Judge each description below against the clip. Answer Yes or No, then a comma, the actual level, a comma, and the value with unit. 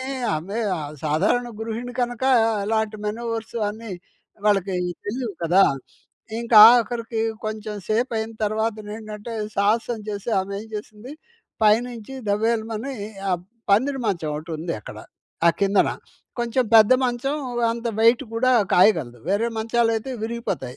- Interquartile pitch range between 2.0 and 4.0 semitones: Yes, narrow, 2.5 semitones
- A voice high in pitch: Yes, high, 220 Hz